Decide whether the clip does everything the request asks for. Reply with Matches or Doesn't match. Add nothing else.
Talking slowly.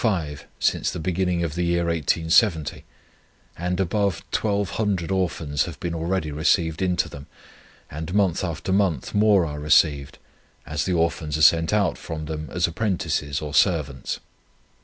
Doesn't match